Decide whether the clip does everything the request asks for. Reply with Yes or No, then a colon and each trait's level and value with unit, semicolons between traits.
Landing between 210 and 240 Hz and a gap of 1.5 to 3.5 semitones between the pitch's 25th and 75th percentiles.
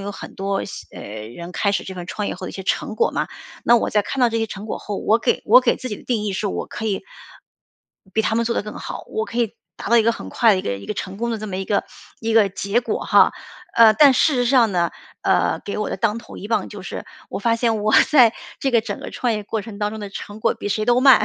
Yes: high, 215 Hz; average, 2.7 semitones